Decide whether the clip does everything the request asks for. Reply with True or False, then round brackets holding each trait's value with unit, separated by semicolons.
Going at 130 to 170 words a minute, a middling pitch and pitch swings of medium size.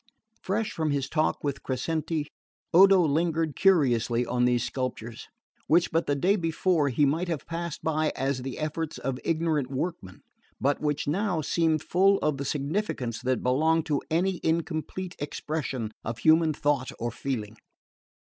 True (155 wpm; 155 Hz; 3.8 semitones)